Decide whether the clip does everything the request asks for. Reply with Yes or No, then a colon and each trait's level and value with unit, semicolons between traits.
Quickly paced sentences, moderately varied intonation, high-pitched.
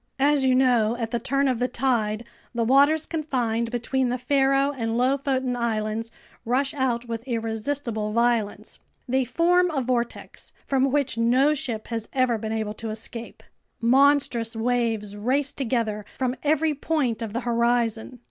No: average, 155 wpm; average, 3.0 semitones; high, 245 Hz